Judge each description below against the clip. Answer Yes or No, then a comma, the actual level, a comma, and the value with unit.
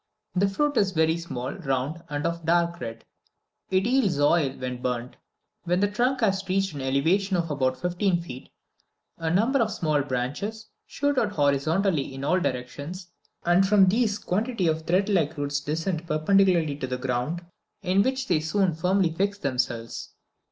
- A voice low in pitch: No, medium, 170 Hz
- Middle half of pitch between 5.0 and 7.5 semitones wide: Yes, wide, 5.5 semitones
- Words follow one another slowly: No, average, 165 wpm